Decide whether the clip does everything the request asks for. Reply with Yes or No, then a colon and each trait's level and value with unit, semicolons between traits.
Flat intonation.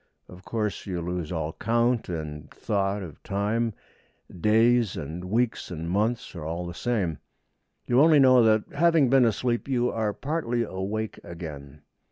No: wide, 5.5 semitones